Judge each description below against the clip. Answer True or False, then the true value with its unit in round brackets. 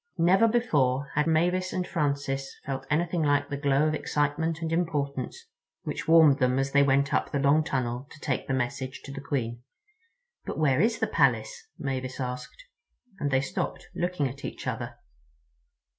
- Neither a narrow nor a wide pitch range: True (3.2 semitones)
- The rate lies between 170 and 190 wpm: True (175 wpm)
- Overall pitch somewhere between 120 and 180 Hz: True (140 Hz)